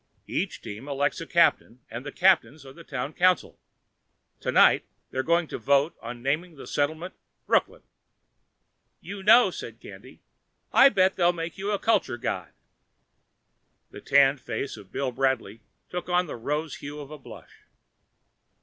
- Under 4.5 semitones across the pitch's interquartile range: No, average, 4.8 semitones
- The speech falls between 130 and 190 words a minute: Yes, average, 155 wpm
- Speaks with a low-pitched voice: No, medium, 150 Hz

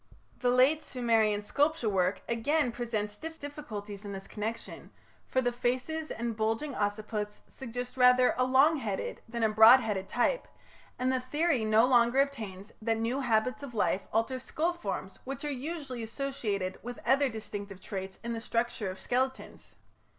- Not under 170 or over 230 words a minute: No, average, 160 wpm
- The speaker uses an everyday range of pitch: Yes, average, 3.7 semitones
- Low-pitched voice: No, high, 235 Hz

